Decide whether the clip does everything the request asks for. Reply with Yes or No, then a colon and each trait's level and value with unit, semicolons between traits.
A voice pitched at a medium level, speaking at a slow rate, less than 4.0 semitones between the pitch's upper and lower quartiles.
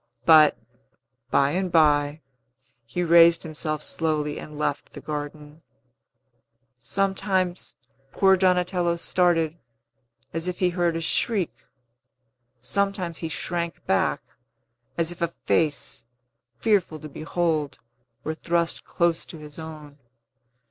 Yes: medium, 165 Hz; slow, 115 wpm; narrow, 2.6 semitones